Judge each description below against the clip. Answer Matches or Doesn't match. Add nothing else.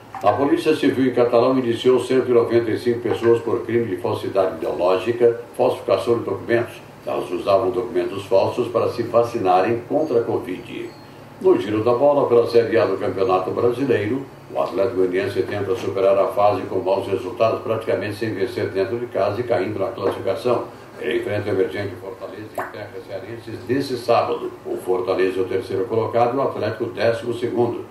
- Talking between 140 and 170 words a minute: Matches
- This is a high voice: Doesn't match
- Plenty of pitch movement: Doesn't match